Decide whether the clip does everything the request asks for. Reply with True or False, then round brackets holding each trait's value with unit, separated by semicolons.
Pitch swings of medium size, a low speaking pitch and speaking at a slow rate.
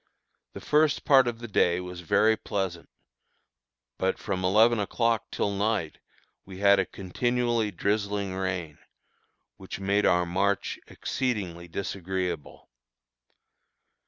True (3.3 semitones; 100 Hz; 115 wpm)